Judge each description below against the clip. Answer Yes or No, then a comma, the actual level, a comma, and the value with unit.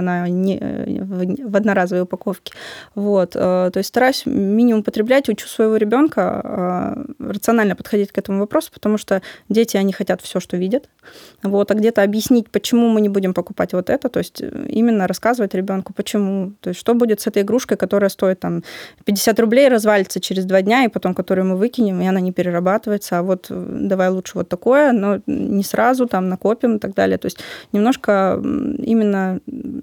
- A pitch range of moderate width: Yes, average, 3.5 semitones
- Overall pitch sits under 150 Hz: No, high, 205 Hz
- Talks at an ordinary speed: No, fast, 175 wpm